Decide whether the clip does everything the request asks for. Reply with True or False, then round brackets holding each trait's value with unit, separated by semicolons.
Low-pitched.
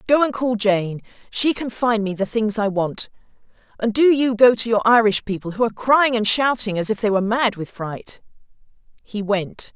False (220 Hz)